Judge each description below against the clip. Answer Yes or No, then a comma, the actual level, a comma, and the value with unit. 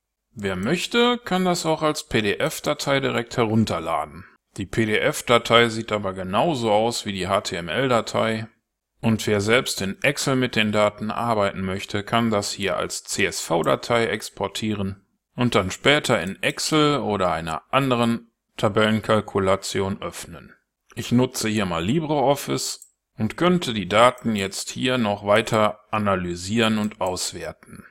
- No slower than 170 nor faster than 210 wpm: No, average, 130 wpm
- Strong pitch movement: No, average, 3.5 semitones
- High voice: No, low, 110 Hz